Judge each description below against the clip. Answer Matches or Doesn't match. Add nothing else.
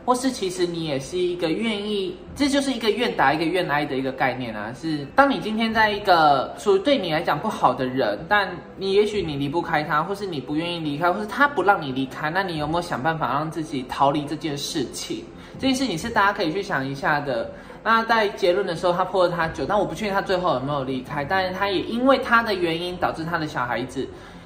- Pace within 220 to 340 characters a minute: Doesn't match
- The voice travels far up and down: Matches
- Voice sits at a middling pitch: Matches